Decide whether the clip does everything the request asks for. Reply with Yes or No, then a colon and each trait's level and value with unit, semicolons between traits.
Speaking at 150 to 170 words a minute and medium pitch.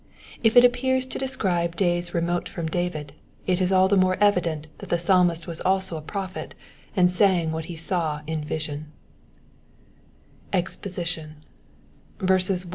No: average, 140 wpm; medium, 175 Hz